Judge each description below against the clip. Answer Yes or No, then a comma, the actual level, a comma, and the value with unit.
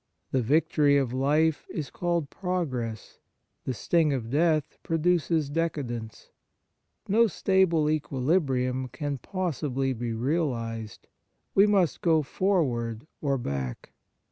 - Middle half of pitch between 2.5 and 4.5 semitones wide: No, average, 4.9 semitones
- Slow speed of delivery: Yes, slow, 110 wpm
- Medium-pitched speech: Yes, medium, 145 Hz